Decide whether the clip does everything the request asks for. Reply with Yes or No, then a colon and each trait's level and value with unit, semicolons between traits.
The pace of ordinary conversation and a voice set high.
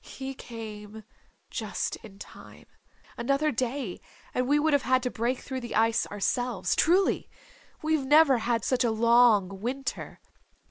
Yes: average, 145 wpm; high, 245 Hz